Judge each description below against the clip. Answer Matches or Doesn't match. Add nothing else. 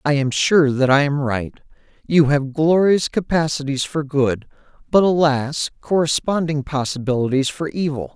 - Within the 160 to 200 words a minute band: Doesn't match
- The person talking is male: Matches